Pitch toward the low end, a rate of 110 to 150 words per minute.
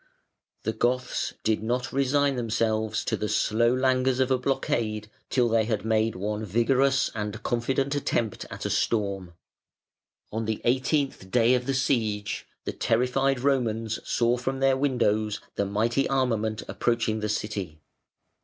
Yes: low, 115 Hz; average, 145 wpm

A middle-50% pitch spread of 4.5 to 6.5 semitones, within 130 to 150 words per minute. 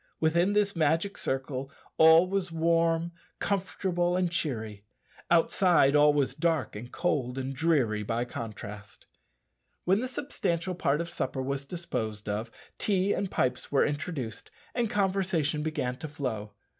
Yes: wide, 5.5 semitones; average, 140 wpm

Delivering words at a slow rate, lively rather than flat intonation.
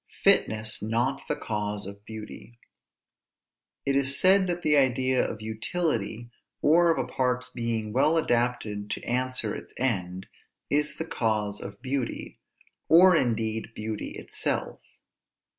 No: slow, 130 wpm; average, 4.2 semitones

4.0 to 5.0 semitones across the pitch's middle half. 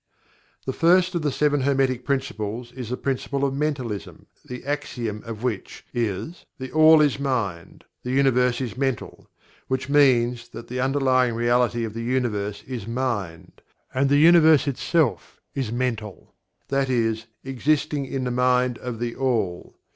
No: average, 2.8 semitones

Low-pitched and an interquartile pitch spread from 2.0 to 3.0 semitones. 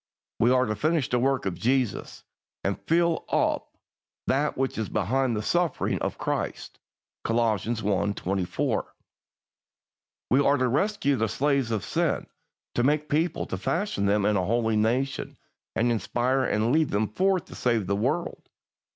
No: low, 120 Hz; average, 4.7 semitones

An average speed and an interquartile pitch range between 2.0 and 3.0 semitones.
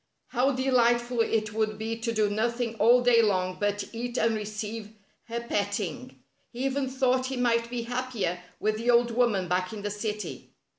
Yes: average, 185 wpm; narrow, 2.6 semitones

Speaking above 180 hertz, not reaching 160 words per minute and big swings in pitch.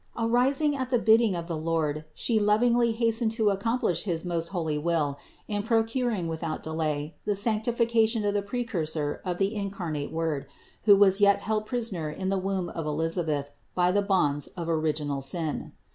No: high, 190 Hz; average, 175 wpm; wide, 5.7 semitones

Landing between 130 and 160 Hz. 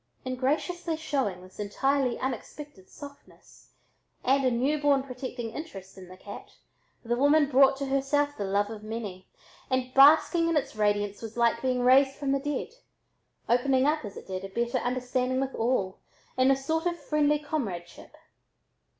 No: very high, 260 Hz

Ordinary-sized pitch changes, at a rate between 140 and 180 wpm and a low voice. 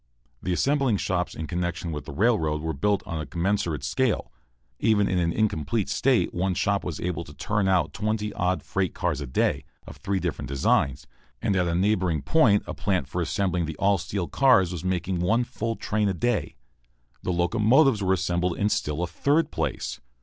No: average, 3.7 semitones; average, 195 wpm; very low, 95 Hz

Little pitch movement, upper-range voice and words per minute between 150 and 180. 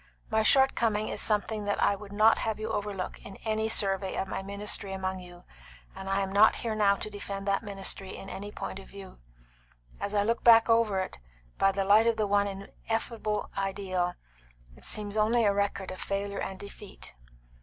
No: narrow, 1.8 semitones; high, 200 Hz; average, 195 wpm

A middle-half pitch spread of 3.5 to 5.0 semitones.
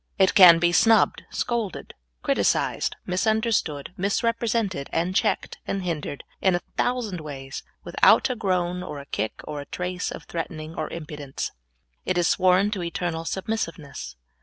Yes: average, 4.0 semitones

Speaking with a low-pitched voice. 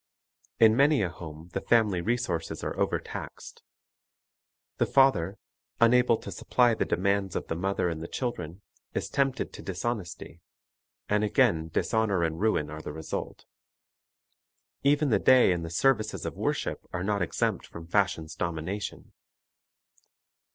Yes: low, 100 Hz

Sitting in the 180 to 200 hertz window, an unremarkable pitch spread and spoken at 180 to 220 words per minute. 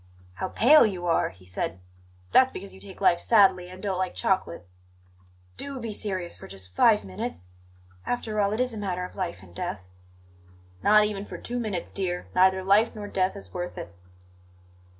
Yes: high, 190 Hz; average, 3.5 semitones; average, 190 wpm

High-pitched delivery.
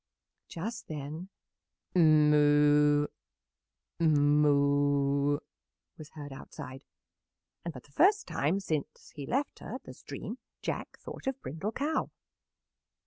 No: medium, 150 Hz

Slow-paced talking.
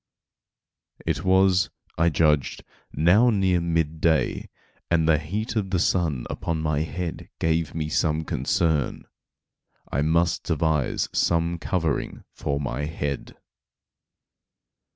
Yes: slow, 115 wpm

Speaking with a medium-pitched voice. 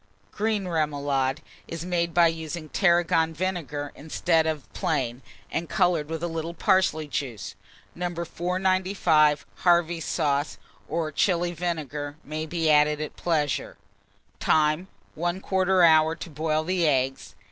Yes: medium, 160 Hz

